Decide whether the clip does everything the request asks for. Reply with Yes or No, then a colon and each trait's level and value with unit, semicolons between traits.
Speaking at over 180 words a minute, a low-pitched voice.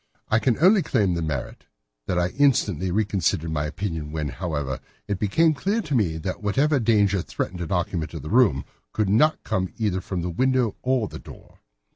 Yes: average, 190 wpm; low, 100 Hz